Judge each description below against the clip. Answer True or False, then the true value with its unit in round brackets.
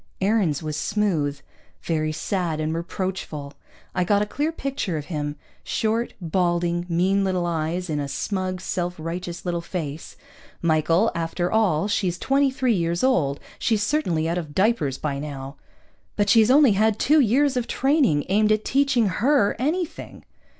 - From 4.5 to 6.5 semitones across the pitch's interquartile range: True (5.5 semitones)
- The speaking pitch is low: False (180 Hz)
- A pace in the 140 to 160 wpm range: True (155 wpm)